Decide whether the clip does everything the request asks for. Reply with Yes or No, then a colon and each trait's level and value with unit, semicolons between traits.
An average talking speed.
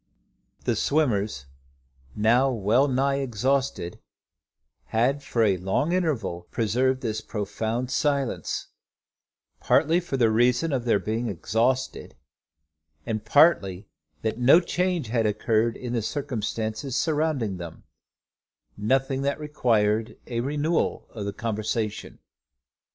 No: slow, 110 wpm